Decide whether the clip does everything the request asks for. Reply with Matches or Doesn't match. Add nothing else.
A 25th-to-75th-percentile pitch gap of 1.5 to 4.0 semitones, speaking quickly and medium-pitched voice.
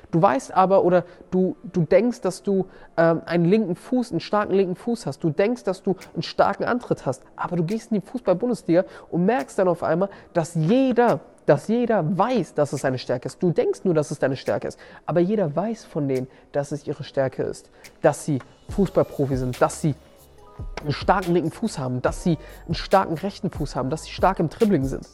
Doesn't match